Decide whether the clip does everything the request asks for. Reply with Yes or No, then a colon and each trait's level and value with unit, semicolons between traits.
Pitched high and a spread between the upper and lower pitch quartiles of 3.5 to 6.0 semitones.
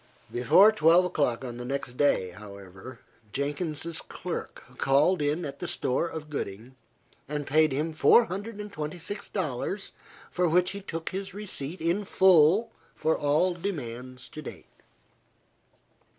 No: medium, 155 Hz; wide, 5.4 semitones